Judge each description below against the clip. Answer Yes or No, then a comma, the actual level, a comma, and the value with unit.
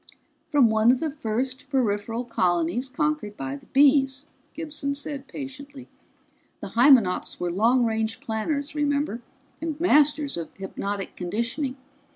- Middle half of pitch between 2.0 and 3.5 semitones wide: No, average, 4.7 semitones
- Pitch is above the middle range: Yes, very high, 260 Hz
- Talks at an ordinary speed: No, slow, 130 wpm